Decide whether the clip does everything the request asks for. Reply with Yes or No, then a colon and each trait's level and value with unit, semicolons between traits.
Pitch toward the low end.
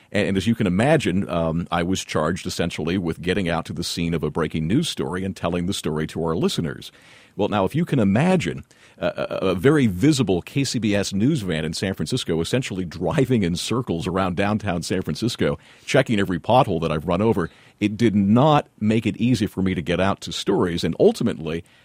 Yes: very low, 95 Hz